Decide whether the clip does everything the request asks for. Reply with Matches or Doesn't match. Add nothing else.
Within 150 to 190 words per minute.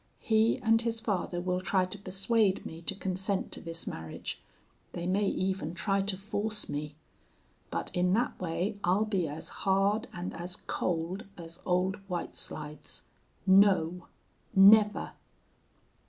Doesn't match